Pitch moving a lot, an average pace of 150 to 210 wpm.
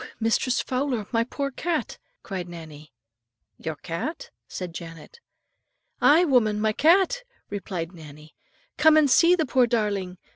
No: wide, 8.9 semitones; slow, 135 wpm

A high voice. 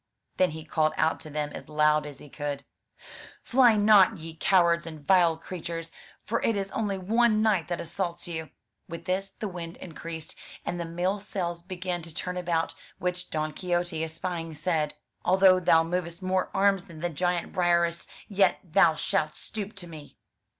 No: medium, 175 Hz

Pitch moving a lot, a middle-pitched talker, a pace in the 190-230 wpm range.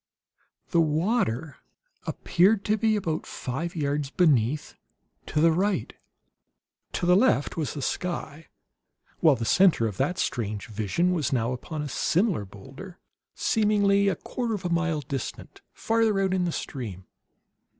No: wide, 6.3 semitones; medium, 165 Hz; average, 145 wpm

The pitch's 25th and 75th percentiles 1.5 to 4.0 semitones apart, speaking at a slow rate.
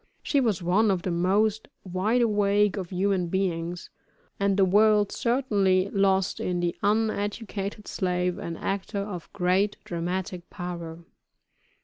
Yes: narrow, 2.5 semitones; slow, 130 wpm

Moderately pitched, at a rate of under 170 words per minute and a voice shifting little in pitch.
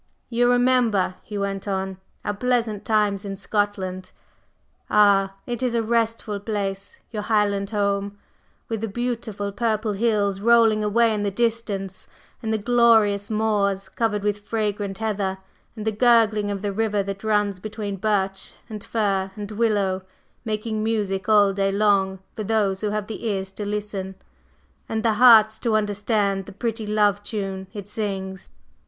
No: high, 210 Hz; average, 155 wpm; narrow, 1.9 semitones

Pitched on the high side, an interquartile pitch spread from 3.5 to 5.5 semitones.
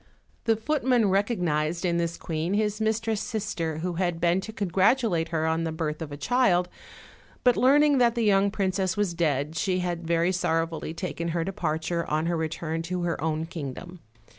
No: medium, 175 Hz; average, 4.0 semitones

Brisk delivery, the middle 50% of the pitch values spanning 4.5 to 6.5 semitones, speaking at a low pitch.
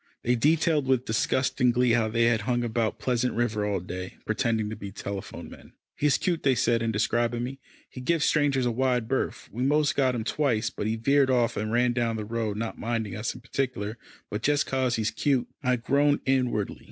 No: fast, 210 wpm; average, 3.0 semitones; low, 120 Hz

